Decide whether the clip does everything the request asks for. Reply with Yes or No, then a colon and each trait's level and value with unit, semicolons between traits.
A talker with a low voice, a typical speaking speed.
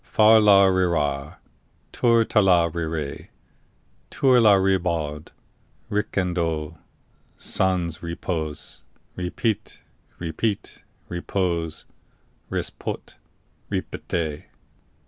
No: very low, 90 Hz; slow, 70 wpm